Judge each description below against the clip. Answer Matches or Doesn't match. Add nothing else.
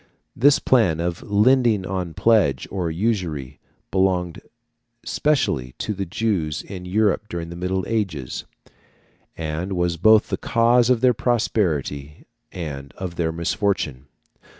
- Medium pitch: Doesn't match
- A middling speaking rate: Doesn't match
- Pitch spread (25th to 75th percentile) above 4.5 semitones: Matches